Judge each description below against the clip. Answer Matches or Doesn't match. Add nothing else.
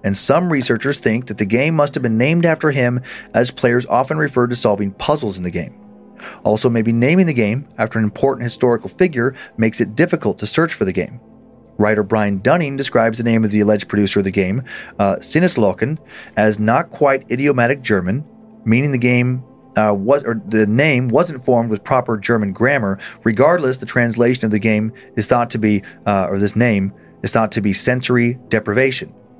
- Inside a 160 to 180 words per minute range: Doesn't match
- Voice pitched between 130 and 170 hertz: Doesn't match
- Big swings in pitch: Doesn't match